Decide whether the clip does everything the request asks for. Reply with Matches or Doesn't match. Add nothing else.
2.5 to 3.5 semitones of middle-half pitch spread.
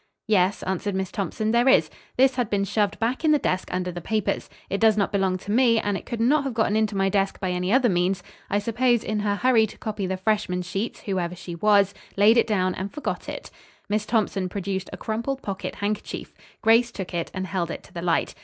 Matches